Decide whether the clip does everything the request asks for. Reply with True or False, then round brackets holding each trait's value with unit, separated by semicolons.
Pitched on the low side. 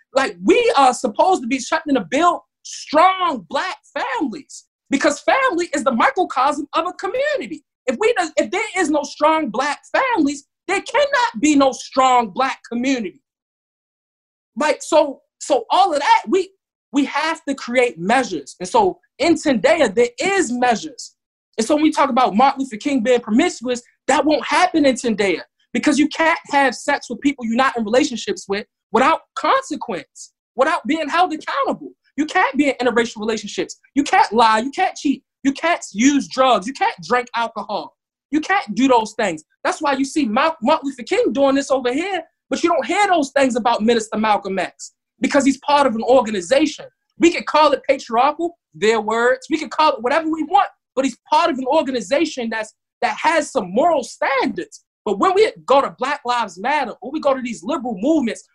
False (280 Hz)